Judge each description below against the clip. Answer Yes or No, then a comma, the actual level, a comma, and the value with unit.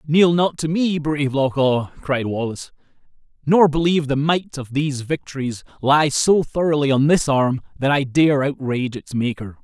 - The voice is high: No, medium, 145 Hz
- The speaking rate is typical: Yes, average, 175 wpm